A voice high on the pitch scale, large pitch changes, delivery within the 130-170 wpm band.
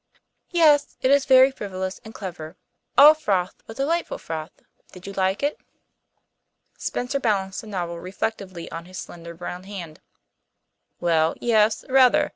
Yes: high, 195 Hz; wide, 6.6 semitones; average, 140 wpm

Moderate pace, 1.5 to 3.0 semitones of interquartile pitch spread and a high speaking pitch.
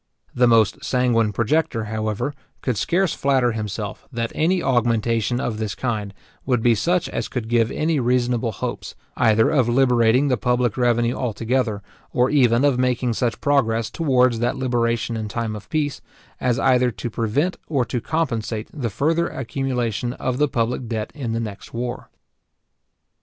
No: average, 160 wpm; narrow, 2.5 semitones; low, 120 Hz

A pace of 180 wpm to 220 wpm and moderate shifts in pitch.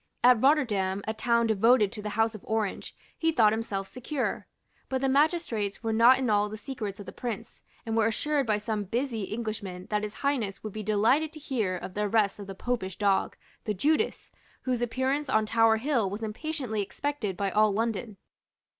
Yes: average, 195 wpm; average, 3.6 semitones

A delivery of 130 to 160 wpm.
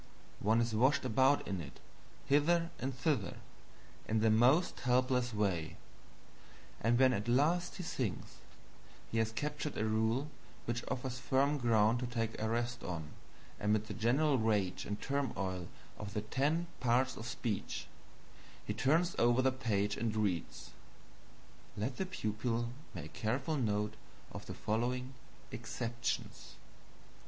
Yes: average, 140 wpm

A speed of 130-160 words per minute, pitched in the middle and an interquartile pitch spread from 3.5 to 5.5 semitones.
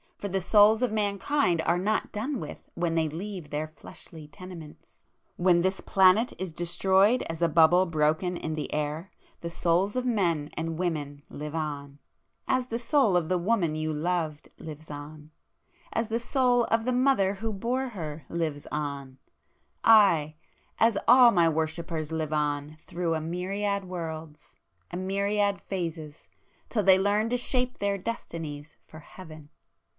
Yes: average, 150 wpm; medium, 175 Hz; average, 4.7 semitones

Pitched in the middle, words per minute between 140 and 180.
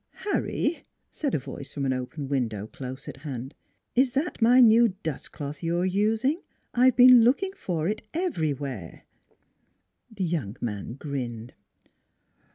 Yes: medium, 165 Hz; average, 150 wpm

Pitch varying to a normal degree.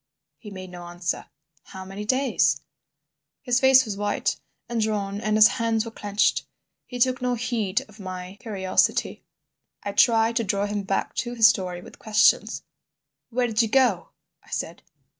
Yes: average, 3.3 semitones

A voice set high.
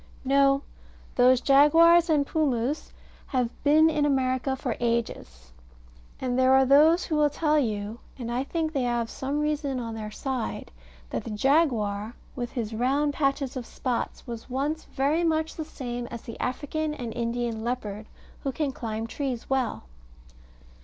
Yes: very high, 260 Hz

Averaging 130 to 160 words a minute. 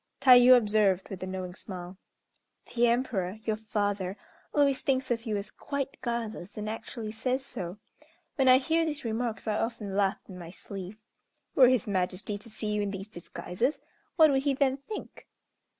No: average, 175 wpm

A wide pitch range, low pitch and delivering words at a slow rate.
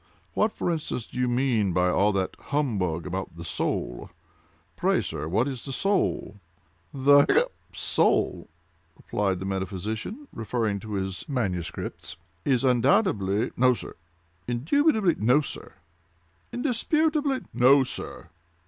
Yes: wide, 7.0 semitones; low, 120 Hz; slow, 120 wpm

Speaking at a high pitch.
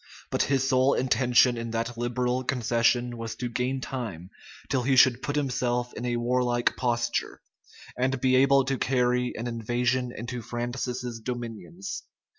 No: low, 125 Hz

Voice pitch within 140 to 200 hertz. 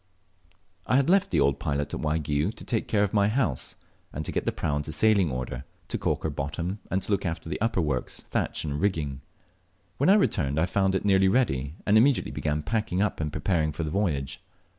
No: very low, 85 Hz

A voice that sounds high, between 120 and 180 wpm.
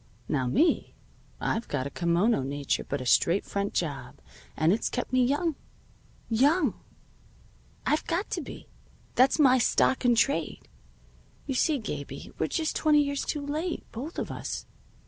Yes: very high, 250 Hz; average, 150 wpm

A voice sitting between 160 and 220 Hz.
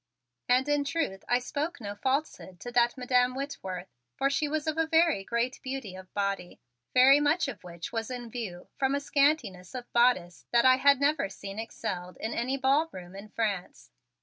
No: high, 245 Hz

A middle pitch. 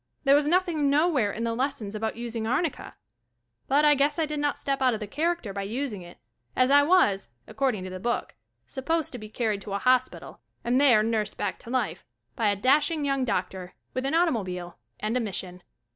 No: very high, 250 Hz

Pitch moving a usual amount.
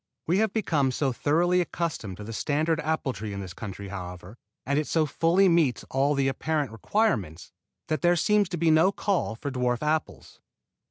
No: wide, 6.8 semitones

